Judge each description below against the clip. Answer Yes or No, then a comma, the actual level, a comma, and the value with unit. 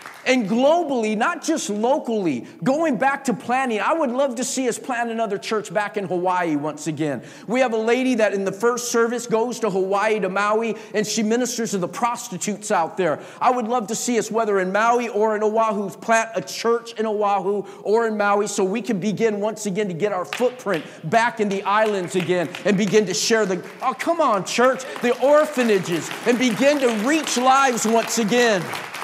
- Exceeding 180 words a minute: Yes, average, 200 wpm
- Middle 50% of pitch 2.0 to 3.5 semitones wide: Yes, average, 3.1 semitones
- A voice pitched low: No, high, 225 Hz